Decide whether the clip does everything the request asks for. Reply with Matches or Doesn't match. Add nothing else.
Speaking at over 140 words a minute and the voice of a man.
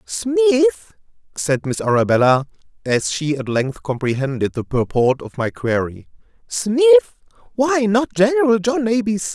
Doesn't match